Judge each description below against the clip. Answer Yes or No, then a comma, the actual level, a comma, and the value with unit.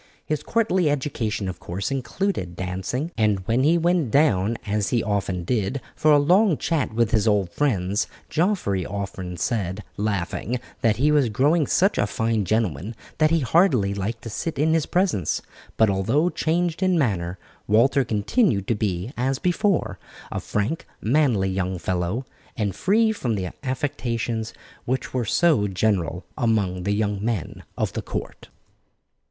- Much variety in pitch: Yes, wide, 7.1 semitones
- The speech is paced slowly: No, average, 160 wpm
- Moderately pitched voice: No, low, 115 Hz